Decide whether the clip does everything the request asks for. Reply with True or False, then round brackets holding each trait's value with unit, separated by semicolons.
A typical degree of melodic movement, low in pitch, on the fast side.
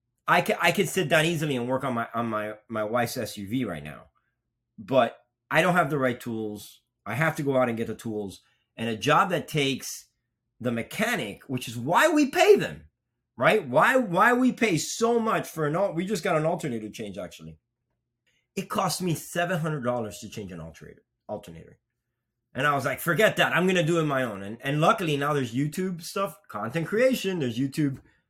False (6.7 semitones; 130 Hz; 210 wpm)